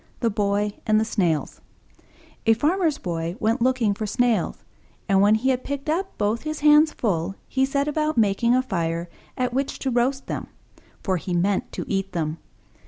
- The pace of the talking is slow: No, average, 180 wpm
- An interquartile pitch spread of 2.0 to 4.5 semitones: No, wide, 5.5 semitones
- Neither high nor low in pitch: No, high, 225 Hz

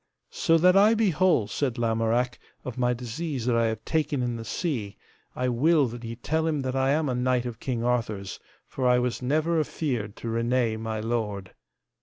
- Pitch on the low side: Yes, low, 125 Hz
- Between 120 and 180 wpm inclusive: No, average, 200 wpm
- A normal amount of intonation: Yes, average, 4.4 semitones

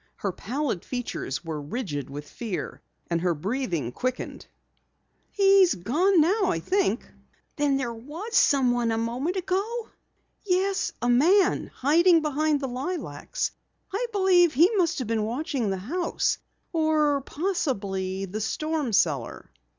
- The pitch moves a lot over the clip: Yes, wide, 8.7 semitones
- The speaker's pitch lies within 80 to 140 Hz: No, very high, 275 Hz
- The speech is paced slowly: Yes, slow, 130 wpm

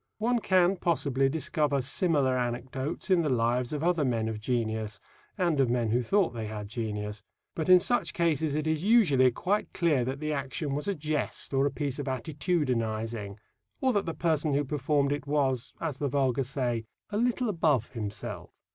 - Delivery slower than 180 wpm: No, average, 185 wpm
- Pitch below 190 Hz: Yes, medium, 140 Hz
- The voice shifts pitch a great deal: No, average, 4.9 semitones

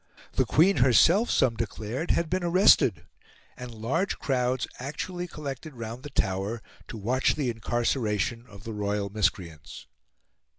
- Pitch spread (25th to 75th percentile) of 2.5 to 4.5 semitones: No, wide, 5.5 semitones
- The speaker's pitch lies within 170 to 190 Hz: No, low, 120 Hz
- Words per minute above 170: No, slow, 135 wpm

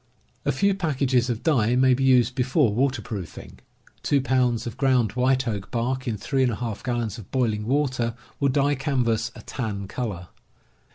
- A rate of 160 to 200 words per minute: Yes, average, 165 wpm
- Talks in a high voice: No, low, 125 Hz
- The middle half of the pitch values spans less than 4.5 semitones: Yes, average, 2.9 semitones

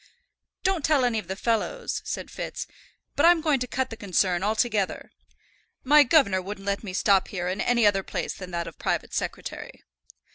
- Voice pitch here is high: Yes, high, 215 Hz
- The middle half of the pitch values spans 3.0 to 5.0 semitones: No, wide, 5.6 semitones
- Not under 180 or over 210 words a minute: Yes, average, 185 wpm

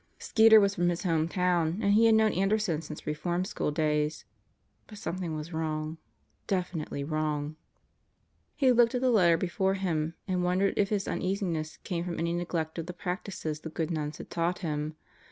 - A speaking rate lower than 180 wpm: No, average, 190 wpm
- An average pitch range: Yes, average, 3.7 semitones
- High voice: No, medium, 175 Hz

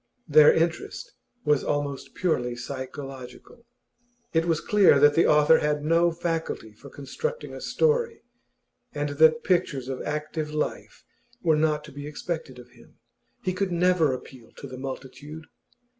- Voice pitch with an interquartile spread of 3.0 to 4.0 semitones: Yes, average, 3.5 semitones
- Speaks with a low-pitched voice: No, medium, 150 Hz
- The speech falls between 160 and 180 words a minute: No, average, 145 wpm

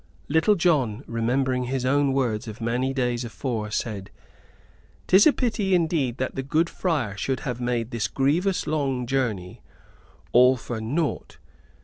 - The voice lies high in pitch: No, low, 130 Hz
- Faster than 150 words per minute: No, average, 145 wpm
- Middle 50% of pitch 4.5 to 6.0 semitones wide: No, average, 4.1 semitones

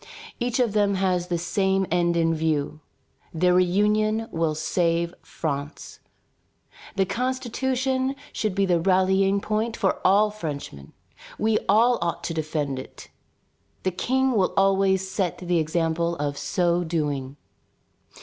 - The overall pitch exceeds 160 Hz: Yes, medium, 185 Hz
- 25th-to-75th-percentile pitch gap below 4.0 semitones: No, average, 4.3 semitones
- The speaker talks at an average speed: No, slow, 130 wpm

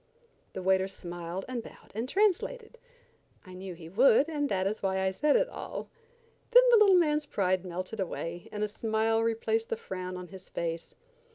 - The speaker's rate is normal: Yes, average, 185 wpm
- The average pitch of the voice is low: No, high, 205 Hz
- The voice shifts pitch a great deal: Yes, wide, 8.3 semitones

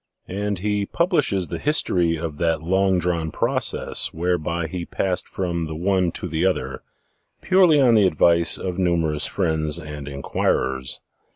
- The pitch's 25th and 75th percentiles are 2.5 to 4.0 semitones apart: Yes, average, 3.1 semitones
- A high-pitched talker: No, very low, 85 Hz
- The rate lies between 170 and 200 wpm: No, average, 155 wpm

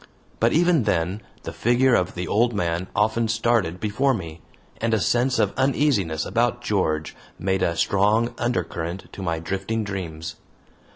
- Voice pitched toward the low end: Yes, low, 105 Hz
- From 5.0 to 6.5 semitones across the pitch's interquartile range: Yes, wide, 5.5 semitones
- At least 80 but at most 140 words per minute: No, average, 155 wpm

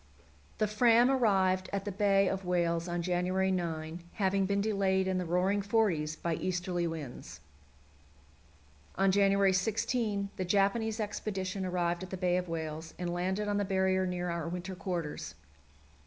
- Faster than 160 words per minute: No, average, 155 wpm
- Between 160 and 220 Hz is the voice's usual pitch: Yes, medium, 185 Hz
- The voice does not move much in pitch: Yes, narrow, 2.2 semitones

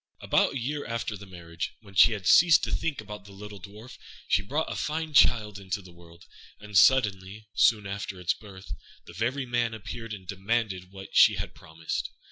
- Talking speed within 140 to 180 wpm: No, average, 195 wpm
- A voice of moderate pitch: No, low, 105 Hz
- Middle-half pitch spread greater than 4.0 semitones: No, average, 3.7 semitones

